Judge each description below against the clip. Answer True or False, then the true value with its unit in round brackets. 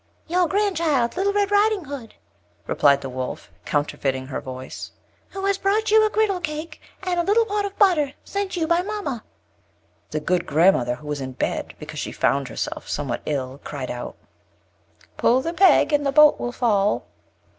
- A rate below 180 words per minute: False (185 wpm)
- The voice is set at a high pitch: True (295 Hz)